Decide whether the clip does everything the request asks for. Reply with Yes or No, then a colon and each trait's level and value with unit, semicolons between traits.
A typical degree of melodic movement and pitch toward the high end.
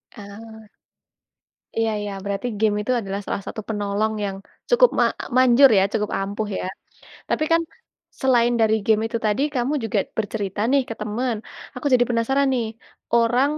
Yes: average, 3.2 semitones; high, 225 Hz